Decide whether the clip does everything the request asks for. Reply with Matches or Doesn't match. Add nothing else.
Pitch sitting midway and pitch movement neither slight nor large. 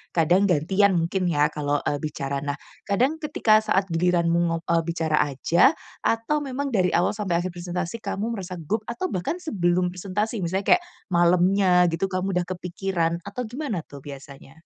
Matches